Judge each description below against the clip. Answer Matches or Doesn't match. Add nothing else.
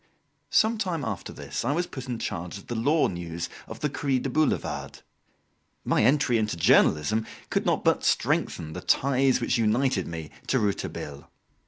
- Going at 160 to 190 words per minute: Matches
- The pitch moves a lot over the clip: Matches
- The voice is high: Doesn't match